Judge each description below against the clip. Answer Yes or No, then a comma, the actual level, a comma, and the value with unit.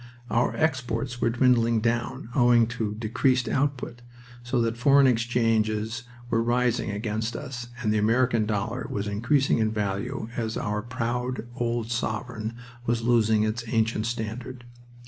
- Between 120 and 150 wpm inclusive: Yes, average, 140 wpm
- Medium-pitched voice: No, low, 115 Hz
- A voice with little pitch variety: Yes, narrow, 2.0 semitones